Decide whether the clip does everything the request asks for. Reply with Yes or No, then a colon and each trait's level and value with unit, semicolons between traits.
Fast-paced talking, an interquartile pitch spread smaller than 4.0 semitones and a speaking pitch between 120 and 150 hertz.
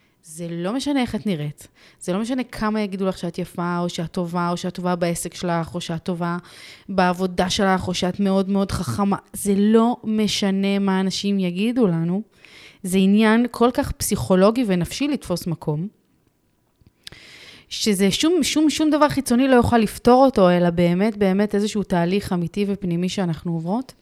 No: fast, 165 wpm; average, 3.4 semitones; high, 195 Hz